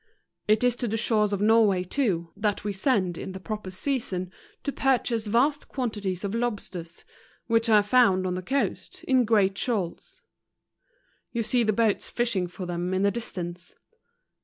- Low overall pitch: No, high, 210 Hz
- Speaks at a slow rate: No, average, 165 wpm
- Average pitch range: Yes, average, 4.1 semitones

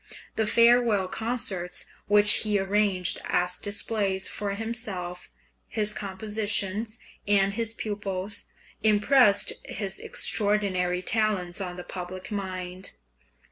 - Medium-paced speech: No, slow, 100 wpm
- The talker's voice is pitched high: Yes, high, 205 Hz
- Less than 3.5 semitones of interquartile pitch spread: Yes, narrow, 2.4 semitones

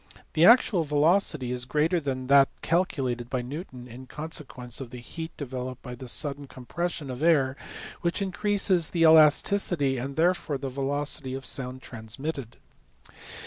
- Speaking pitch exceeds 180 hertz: No, medium, 140 Hz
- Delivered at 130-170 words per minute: Yes, average, 155 wpm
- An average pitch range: Yes, average, 4.2 semitones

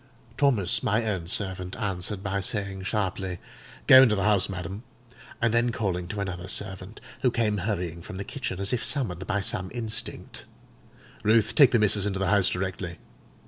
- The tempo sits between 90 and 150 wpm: No, average, 170 wpm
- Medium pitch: No, low, 100 Hz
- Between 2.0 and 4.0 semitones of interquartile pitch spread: Yes, average, 2.7 semitones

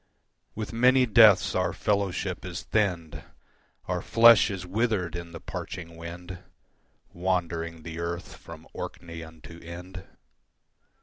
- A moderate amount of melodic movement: Yes, average, 3.4 semitones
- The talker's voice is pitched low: Yes, very low, 90 Hz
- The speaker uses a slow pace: Yes, slow, 120 wpm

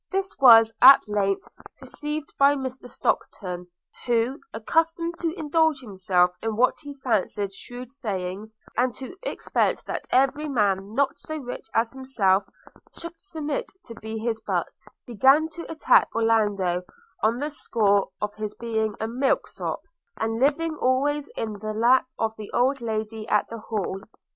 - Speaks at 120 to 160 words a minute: Yes, average, 155 wpm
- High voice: Yes, high, 235 Hz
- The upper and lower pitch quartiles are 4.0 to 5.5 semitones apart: Yes, average, 4.7 semitones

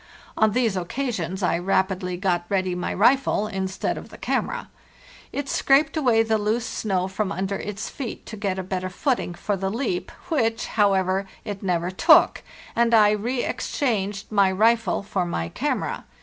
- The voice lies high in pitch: Yes, high, 200 Hz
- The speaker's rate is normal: Yes, average, 165 wpm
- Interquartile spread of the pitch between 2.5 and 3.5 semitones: Yes, average, 3.2 semitones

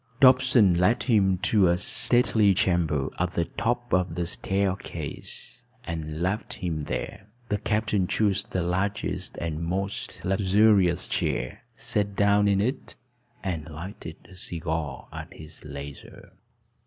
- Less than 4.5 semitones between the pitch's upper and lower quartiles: Yes, average, 3.4 semitones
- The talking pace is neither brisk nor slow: No, slow, 130 wpm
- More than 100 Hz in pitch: No, very low, 95 Hz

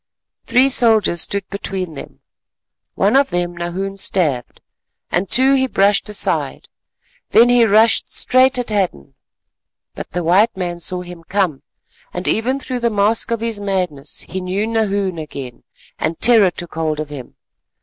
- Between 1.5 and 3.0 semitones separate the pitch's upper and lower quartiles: No, average, 4.5 semitones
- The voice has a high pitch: Yes, high, 195 Hz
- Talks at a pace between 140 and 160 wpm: Yes, average, 155 wpm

